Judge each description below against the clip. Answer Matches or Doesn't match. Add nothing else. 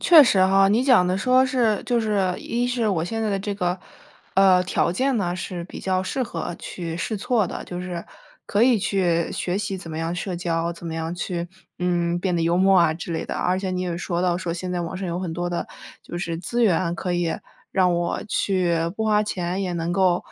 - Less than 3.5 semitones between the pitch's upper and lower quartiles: Matches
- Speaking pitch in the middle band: Matches